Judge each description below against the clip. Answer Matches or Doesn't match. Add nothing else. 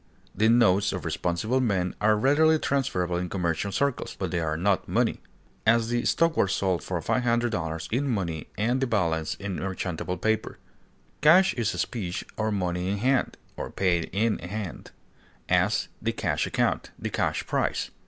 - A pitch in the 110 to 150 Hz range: Doesn't match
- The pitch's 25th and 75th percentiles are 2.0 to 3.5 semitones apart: Doesn't match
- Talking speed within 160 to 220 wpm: Matches